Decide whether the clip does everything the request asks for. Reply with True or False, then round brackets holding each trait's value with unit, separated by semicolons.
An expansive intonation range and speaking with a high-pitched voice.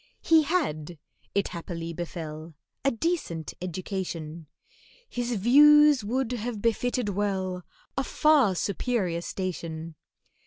True (6.7 semitones; 195 Hz)